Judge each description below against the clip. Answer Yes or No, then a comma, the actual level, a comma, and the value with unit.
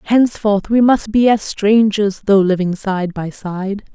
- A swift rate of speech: No, average, 165 wpm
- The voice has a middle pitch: No, high, 205 Hz